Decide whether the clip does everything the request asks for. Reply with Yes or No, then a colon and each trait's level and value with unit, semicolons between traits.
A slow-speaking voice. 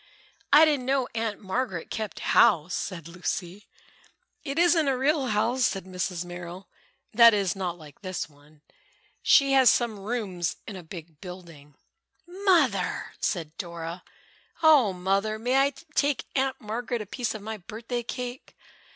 No: average, 150 wpm